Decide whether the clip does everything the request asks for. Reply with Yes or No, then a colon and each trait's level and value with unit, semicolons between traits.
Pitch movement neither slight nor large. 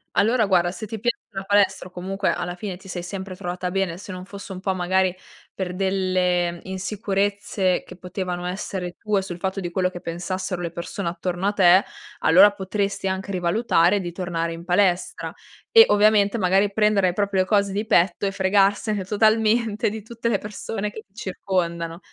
No: narrow, 2.3 semitones